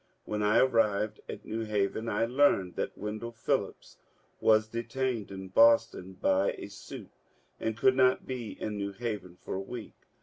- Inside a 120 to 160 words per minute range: No, average, 170 wpm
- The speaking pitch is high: No, low, 110 Hz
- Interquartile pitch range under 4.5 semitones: Yes, average, 2.8 semitones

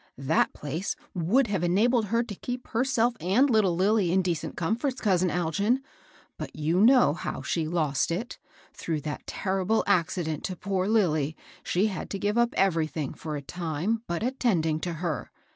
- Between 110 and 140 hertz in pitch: No, medium, 185 Hz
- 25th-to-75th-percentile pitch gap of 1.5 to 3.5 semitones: No, wide, 5.4 semitones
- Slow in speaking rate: No, average, 175 wpm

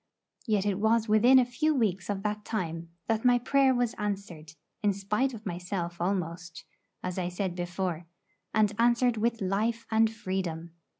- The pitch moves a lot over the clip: No, average, 4.2 semitones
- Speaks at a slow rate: No, average, 165 wpm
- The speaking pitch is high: Yes, high, 205 Hz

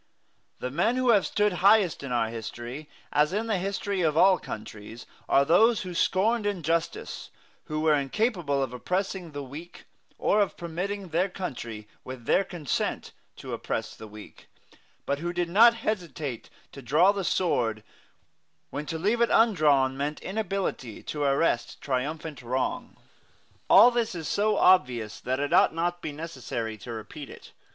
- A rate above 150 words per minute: Yes, average, 160 wpm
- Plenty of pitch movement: Yes, wide, 6.7 semitones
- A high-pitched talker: No, medium, 160 Hz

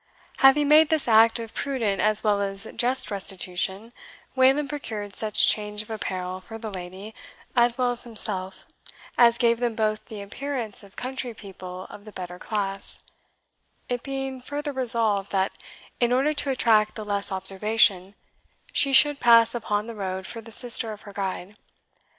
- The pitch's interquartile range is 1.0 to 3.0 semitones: No, average, 3.6 semitones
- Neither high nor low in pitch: No, high, 220 Hz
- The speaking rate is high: No, average, 165 wpm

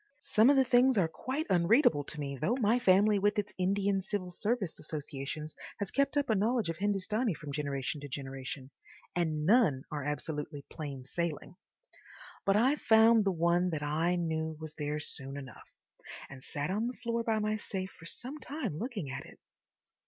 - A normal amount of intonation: No, wide, 6.8 semitones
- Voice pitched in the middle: Yes, medium, 180 Hz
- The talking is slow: No, average, 175 wpm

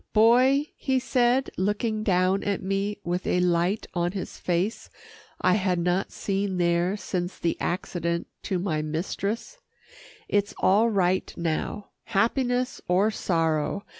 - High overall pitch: Yes, high, 195 Hz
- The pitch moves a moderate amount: Yes, average, 3.6 semitones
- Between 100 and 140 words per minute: Yes, slow, 135 wpm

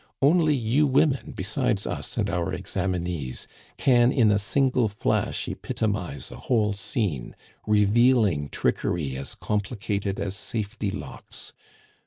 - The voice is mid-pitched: No, low, 105 Hz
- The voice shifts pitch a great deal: No, average, 4.3 semitones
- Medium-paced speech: No, slow, 120 wpm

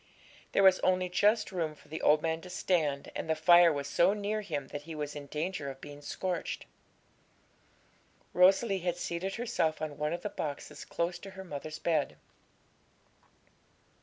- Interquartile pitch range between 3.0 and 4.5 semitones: Yes, average, 3.8 semitones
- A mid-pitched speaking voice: Yes, medium, 170 Hz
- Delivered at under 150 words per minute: No, average, 170 wpm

